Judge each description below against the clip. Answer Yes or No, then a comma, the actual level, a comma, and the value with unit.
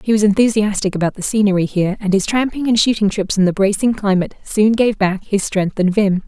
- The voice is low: No, high, 205 Hz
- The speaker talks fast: Yes, fast, 230 wpm